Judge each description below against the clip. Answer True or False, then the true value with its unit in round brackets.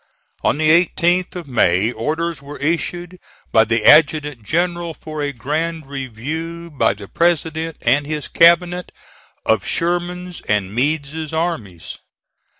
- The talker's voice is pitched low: False (155 Hz)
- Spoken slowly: True (130 wpm)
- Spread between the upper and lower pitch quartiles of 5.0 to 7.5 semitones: False (3.8 semitones)